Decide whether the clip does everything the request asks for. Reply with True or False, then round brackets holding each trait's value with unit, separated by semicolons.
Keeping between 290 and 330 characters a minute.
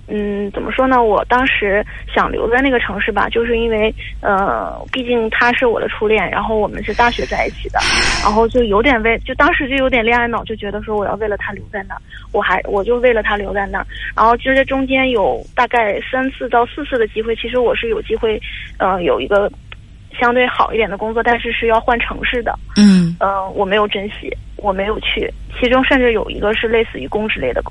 True (325 characters per minute)